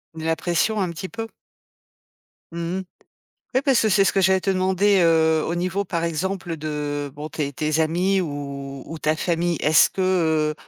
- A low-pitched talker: No, medium, 170 Hz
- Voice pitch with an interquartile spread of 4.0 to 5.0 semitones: No, average, 3.3 semitones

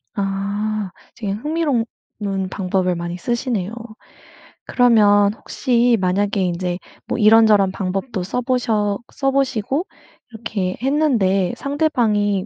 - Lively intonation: No, average, 4.0 semitones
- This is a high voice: Yes, high, 210 Hz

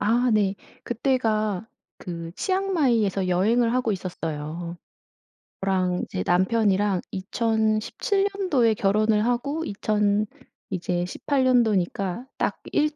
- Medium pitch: No, high, 215 Hz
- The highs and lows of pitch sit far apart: No, average, 4.4 semitones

